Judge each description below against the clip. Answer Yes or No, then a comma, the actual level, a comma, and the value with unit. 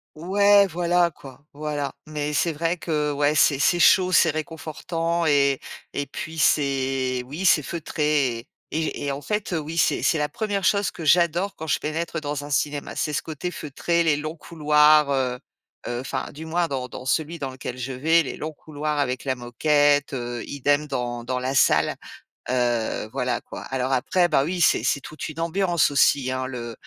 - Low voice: No, medium, 150 Hz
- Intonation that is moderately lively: Yes, average, 3.6 semitones